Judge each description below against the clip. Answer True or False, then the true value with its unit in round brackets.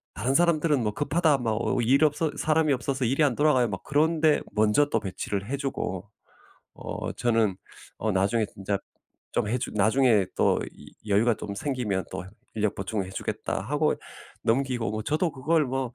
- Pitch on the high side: False (125 Hz)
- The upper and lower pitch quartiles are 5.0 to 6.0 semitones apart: True (5.6 semitones)